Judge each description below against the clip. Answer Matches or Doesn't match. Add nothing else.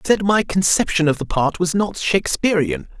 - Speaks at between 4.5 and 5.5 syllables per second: Matches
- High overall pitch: Doesn't match